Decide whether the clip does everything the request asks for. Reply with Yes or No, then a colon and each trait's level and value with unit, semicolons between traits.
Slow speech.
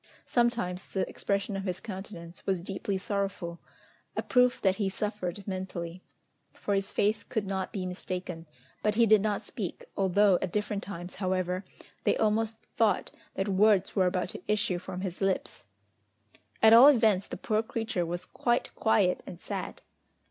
No: average, 165 wpm